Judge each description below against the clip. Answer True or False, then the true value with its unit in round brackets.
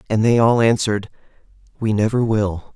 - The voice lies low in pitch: True (110 Hz)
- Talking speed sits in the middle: True (155 wpm)